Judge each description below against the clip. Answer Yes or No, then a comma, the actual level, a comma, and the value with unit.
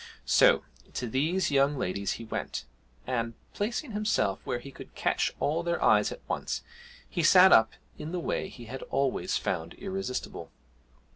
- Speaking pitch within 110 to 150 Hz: Yes, medium, 140 Hz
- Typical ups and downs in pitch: No, wide, 7.7 semitones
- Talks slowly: No, average, 160 wpm